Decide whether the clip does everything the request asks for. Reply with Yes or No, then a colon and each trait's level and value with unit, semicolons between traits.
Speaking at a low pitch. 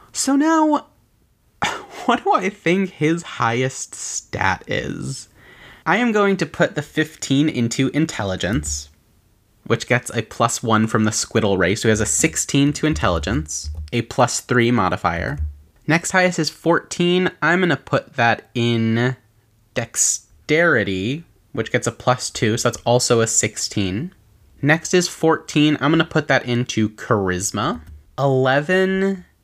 Yes: low, 120 Hz